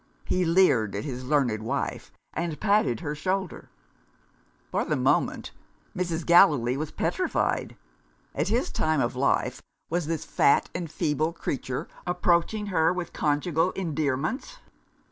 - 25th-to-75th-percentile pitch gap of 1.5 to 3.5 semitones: No, average, 4.2 semitones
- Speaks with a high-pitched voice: No, medium, 160 Hz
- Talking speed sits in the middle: No, slow, 130 wpm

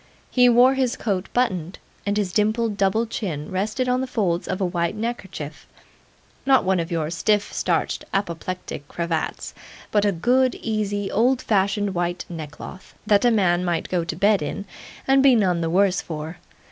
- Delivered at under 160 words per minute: No, average, 170 wpm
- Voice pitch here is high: Yes, high, 195 Hz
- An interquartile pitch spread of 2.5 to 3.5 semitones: No, average, 4.3 semitones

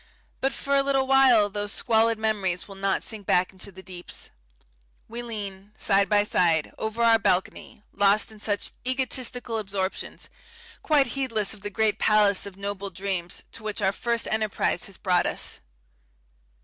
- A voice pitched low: No, high, 210 Hz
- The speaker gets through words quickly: No, average, 160 wpm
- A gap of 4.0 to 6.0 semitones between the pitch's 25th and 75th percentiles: No, average, 2.8 semitones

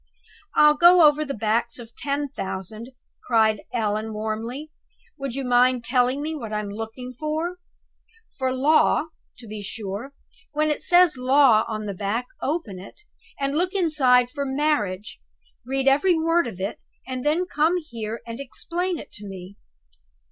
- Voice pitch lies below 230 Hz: No, very high, 255 Hz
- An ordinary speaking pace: Yes, average, 160 wpm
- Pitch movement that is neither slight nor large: No, wide, 5.7 semitones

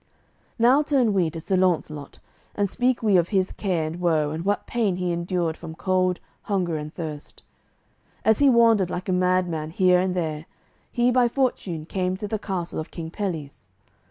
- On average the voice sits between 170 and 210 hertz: Yes, medium, 185 Hz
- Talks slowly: No, average, 185 wpm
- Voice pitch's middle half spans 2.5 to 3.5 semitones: No, average, 3.9 semitones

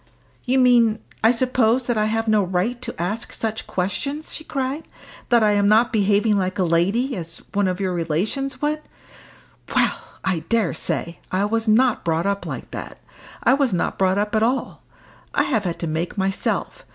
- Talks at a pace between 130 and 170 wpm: No, average, 190 wpm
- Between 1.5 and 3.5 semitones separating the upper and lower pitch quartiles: No, average, 4.6 semitones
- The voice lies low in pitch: No, high, 215 Hz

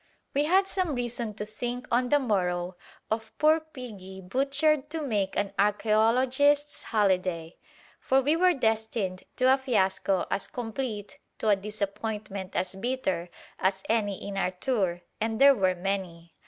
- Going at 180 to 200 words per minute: No, average, 150 wpm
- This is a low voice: No, high, 220 Hz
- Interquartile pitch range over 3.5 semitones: Yes, average, 5.3 semitones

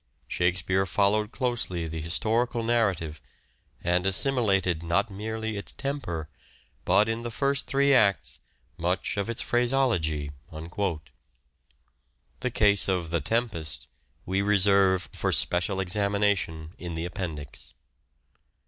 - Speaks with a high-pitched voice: No, very low, 95 Hz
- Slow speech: Yes, slow, 110 wpm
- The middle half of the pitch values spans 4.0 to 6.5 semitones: Yes, average, 5.0 semitones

